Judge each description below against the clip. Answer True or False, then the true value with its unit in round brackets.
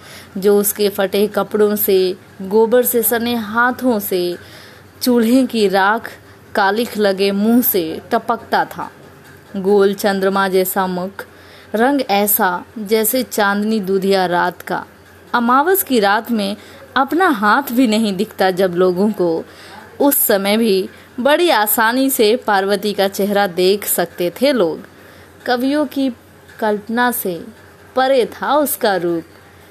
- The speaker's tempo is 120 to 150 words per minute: True (125 wpm)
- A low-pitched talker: False (210 Hz)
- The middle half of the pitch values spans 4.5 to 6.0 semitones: False (3.7 semitones)